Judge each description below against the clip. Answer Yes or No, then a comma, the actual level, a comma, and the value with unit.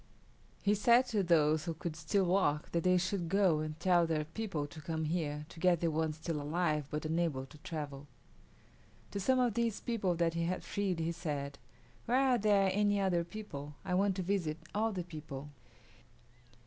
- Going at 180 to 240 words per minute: Yes, average, 190 wpm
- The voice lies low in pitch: No, medium, 170 Hz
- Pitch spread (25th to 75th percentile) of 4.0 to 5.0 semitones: Yes, average, 4.3 semitones